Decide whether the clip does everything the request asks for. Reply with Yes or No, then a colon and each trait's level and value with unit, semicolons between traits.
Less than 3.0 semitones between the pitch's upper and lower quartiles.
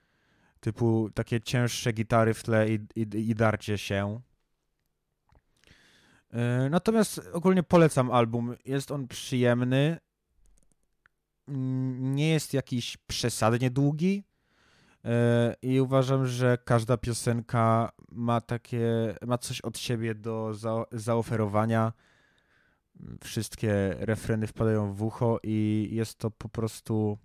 Yes: narrow, 2.5 semitones